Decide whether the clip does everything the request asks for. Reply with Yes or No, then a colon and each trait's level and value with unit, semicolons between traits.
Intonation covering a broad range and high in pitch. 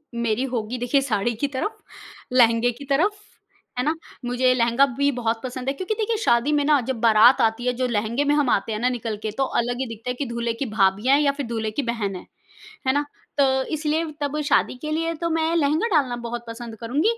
No: average, 3.8 semitones; very high, 250 Hz